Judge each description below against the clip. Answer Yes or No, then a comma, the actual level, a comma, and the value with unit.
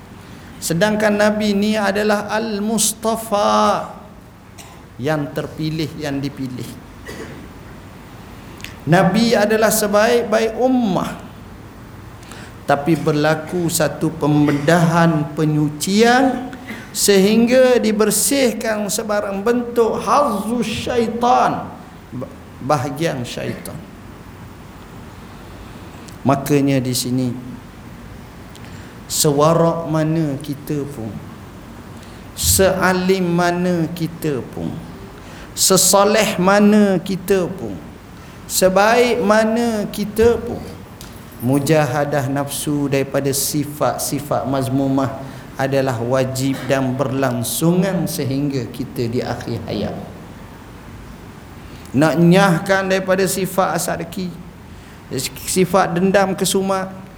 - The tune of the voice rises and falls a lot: Yes, wide, 7.2 semitones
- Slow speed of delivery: Yes, slow, 70 wpm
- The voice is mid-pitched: Yes, medium, 160 Hz